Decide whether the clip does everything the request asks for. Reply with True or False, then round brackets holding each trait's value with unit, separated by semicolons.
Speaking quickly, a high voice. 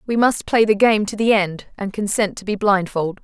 True (240 wpm; 205 Hz)